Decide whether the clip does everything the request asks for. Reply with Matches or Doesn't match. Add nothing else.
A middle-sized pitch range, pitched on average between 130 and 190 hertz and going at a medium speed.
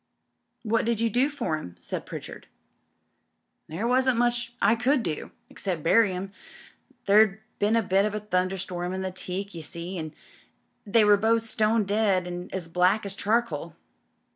Doesn't match